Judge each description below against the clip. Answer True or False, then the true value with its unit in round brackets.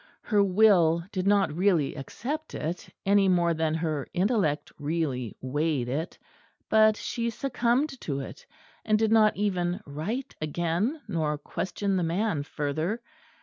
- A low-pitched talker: False (180 Hz)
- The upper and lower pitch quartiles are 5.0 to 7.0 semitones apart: True (5.4 semitones)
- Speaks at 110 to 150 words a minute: True (140 wpm)